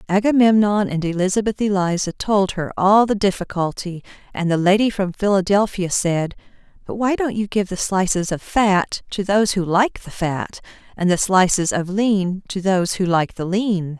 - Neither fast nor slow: Yes, average, 175 wpm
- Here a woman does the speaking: Yes, female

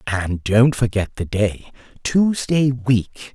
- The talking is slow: Yes, slow, 125 wpm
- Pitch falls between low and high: No, low, 115 Hz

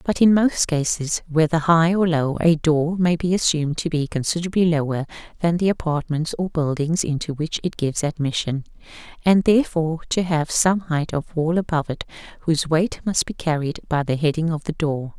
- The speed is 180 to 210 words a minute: Yes, average, 190 wpm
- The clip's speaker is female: Yes, female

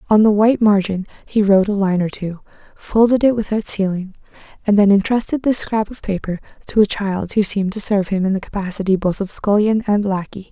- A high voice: Yes, high, 200 Hz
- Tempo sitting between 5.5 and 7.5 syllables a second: Yes, 5.9 syllables/s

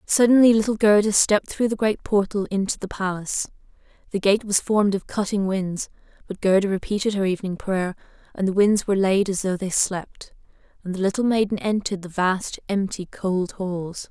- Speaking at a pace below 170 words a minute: No, average, 185 wpm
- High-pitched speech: Yes, high, 195 Hz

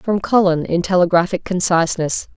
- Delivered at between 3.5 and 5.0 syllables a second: No, 5.3 syllables/s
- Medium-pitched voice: Yes, medium, 180 Hz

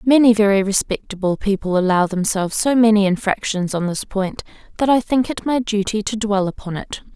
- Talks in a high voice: Yes, high, 205 Hz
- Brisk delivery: No, average, 185 wpm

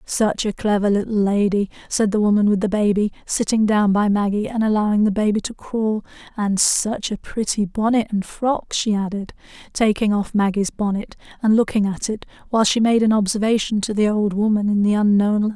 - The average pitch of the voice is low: No, high, 210 Hz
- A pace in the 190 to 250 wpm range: Yes, average, 195 wpm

